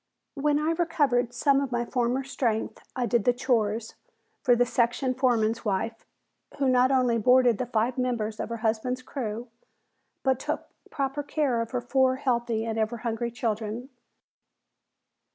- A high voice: Yes, high, 245 Hz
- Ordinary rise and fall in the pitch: No, narrow, 2.3 semitones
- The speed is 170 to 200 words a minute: No, average, 155 wpm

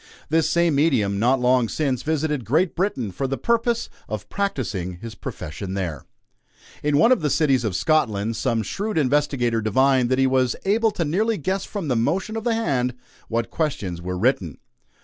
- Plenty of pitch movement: Yes, wide, 6.6 semitones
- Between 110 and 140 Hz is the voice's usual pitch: Yes, low, 135 Hz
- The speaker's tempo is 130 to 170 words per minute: No, average, 180 wpm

